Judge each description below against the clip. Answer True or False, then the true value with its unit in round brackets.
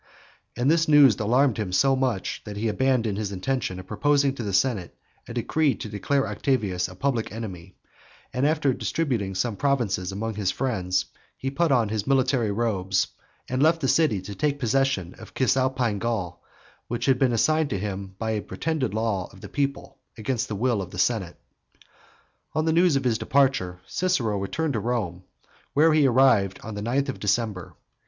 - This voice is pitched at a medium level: False (115 Hz)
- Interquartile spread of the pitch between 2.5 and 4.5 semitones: False (5.3 semitones)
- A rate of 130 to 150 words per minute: False (185 wpm)